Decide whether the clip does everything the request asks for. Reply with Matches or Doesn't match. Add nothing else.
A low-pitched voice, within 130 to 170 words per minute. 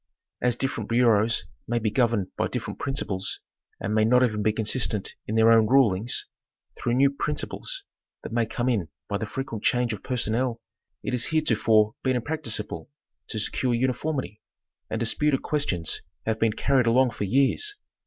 Matches